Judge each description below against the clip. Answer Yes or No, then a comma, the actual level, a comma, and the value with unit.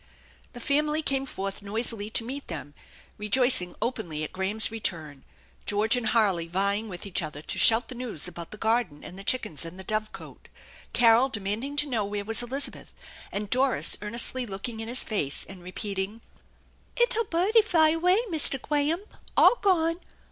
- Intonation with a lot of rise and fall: Yes, wide, 5.7 semitones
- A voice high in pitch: Yes, high, 225 Hz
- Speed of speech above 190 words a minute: No, average, 170 wpm